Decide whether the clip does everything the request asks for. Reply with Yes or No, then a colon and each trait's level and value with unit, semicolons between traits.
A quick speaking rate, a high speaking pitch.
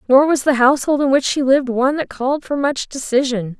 Yes: fast, 235 wpm; very high, 270 Hz